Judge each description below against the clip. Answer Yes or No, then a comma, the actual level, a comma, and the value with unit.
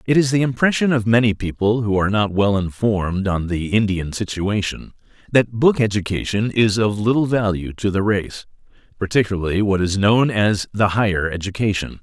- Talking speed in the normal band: Yes, average, 170 wpm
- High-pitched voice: No, low, 105 Hz